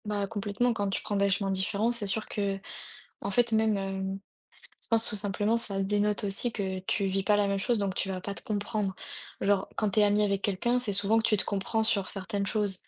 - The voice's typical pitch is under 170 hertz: No, high, 205 Hz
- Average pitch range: No, narrow, 1.7 semitones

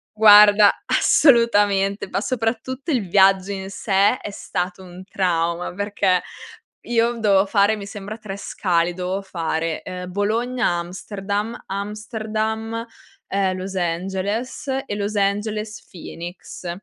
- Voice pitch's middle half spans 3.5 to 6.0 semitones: No, narrow, 2.6 semitones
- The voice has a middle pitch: No, high, 200 Hz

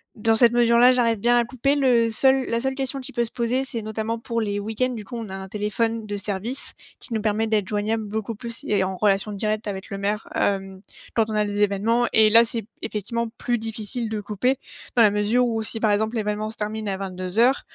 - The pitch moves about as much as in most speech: No, narrow, 2.3 semitones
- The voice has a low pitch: No, high, 220 Hz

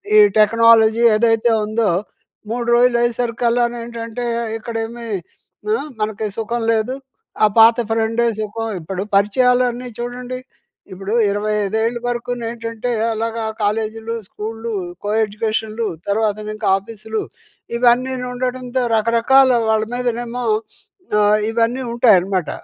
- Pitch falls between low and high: No, high, 230 Hz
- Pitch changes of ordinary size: No, narrow, 1.8 semitones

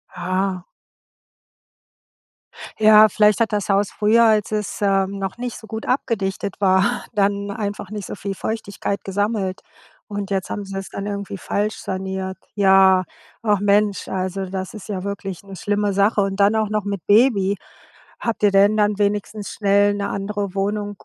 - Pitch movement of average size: No, narrow, 1.4 semitones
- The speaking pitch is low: No, high, 200 Hz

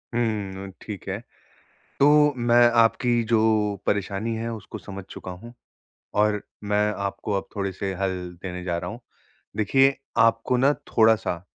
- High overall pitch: No, low, 105 Hz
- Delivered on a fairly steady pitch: No, average, 3.3 semitones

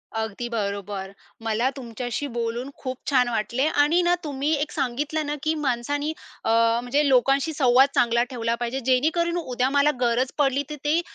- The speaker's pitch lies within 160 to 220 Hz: No, very high, 260 Hz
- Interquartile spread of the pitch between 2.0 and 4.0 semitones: Yes, average, 3.6 semitones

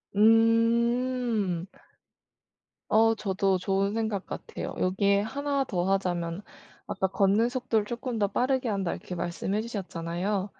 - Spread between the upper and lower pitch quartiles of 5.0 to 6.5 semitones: No, average, 3.3 semitones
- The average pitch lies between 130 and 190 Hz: No, high, 205 Hz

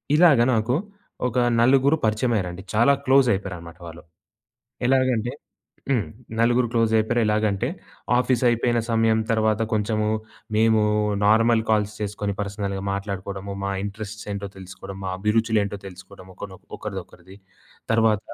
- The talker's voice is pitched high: No, low, 110 Hz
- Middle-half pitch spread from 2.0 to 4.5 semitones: Yes, average, 2.9 semitones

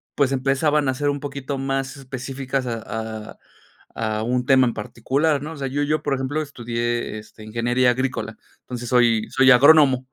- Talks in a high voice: No, low, 130 Hz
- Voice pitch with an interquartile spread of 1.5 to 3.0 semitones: Yes, average, 2.7 semitones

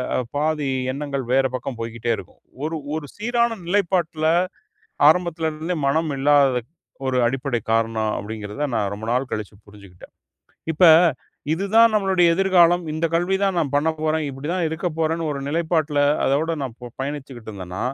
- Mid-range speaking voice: Yes, medium, 150 Hz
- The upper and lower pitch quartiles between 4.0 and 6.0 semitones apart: Yes, average, 5.3 semitones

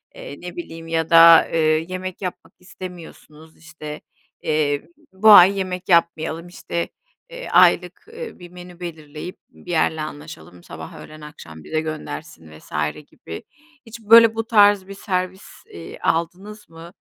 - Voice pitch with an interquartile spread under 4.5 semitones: Yes, average, 3.1 semitones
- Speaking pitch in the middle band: Yes, medium, 170 Hz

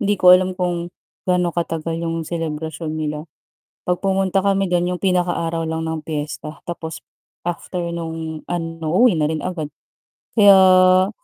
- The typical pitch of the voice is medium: Yes, medium, 170 Hz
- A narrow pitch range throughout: Yes, narrow, 2.3 semitones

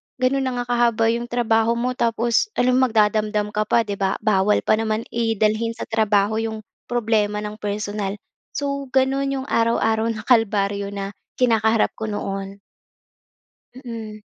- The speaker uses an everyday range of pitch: No, narrow, 2.1 semitones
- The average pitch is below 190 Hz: No, high, 220 Hz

